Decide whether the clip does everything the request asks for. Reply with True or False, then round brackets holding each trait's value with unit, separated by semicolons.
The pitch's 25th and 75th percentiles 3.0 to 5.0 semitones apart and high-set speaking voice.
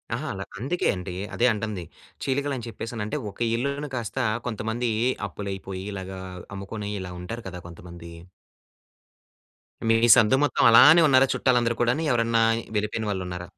False (4.4 semitones; 110 Hz)